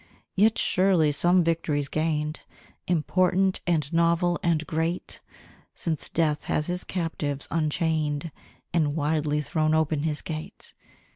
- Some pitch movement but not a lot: No, narrow, 2.2 semitones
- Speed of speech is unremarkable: No, slow, 120 wpm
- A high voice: No, medium, 160 Hz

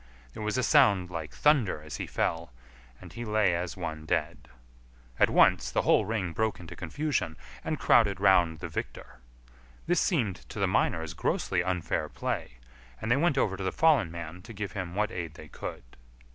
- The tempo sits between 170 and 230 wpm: Yes, average, 185 wpm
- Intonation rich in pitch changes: No, average, 4.6 semitones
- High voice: No, very low, 95 Hz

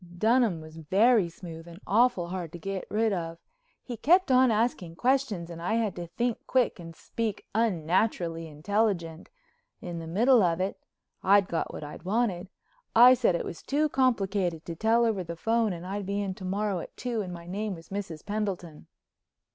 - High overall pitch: Yes, high, 195 Hz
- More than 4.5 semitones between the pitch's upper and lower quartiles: Yes, average, 5.0 semitones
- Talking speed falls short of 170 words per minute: No, average, 180 wpm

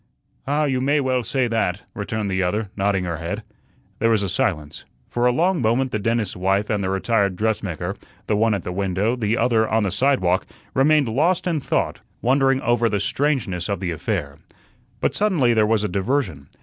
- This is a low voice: Yes, low, 110 Hz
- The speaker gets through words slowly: No, average, 195 wpm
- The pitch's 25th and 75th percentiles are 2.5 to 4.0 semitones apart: No, average, 5.0 semitones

